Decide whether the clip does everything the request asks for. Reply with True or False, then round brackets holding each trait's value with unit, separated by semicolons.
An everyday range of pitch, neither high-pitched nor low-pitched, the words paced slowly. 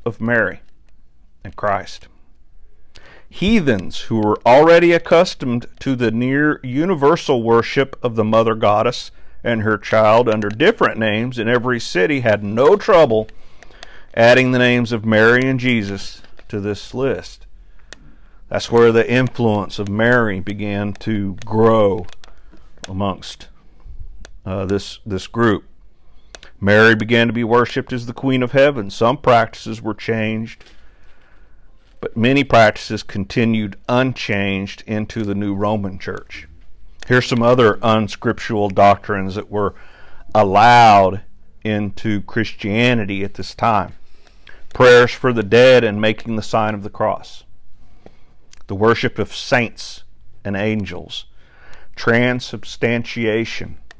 False (3.0 semitones; 110 Hz; 120 wpm)